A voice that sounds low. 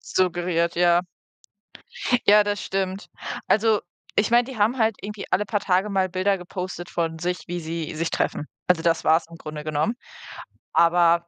No: medium, 180 Hz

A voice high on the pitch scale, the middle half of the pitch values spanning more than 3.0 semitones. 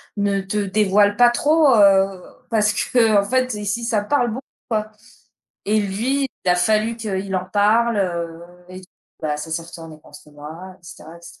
Yes: high, 205 Hz; average, 3.5 semitones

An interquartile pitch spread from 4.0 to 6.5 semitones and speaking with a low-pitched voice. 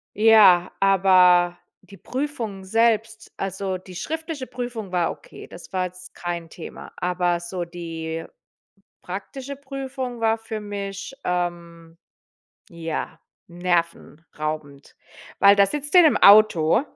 No: average, 4.4 semitones; high, 190 Hz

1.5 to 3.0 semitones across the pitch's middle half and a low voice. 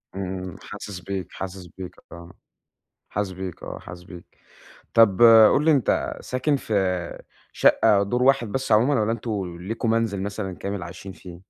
No: average, 3.7 semitones; low, 100 Hz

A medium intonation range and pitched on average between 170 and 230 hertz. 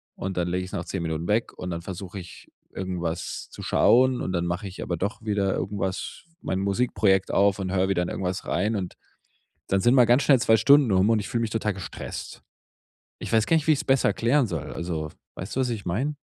No: average, 4.1 semitones; very low, 95 Hz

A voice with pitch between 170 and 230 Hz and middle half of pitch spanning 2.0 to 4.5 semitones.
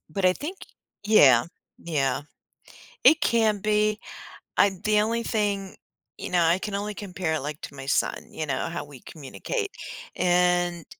No: medium, 185 Hz; average, 5.1 semitones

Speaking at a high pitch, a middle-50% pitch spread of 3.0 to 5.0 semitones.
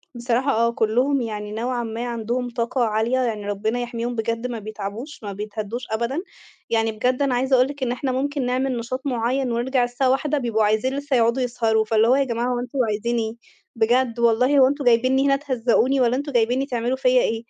No: high, 240 Hz; narrow, 2.4 semitones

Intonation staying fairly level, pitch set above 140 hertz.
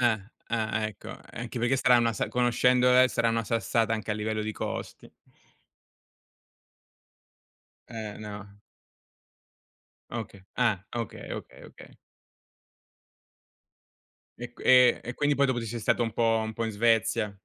No: narrow, 1.9 semitones; low, 115 Hz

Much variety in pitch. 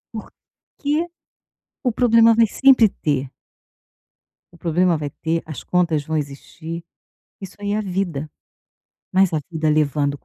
No: average, 4.6 semitones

